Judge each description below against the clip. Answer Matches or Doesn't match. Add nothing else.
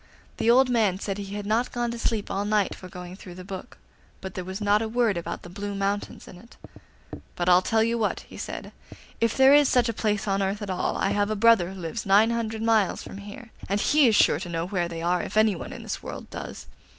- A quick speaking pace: Matches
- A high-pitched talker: Matches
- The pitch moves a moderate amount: Matches